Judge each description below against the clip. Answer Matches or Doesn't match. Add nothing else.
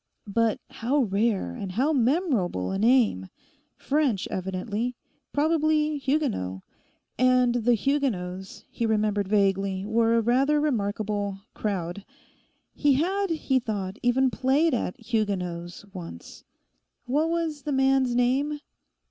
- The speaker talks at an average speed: Doesn't match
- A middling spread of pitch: Doesn't match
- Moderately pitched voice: Doesn't match